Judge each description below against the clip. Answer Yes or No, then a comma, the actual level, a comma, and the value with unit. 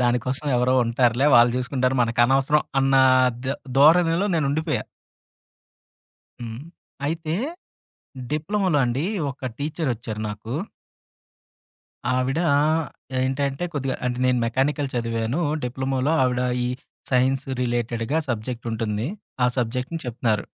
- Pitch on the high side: No, low, 130 Hz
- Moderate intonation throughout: Yes, average, 3.2 semitones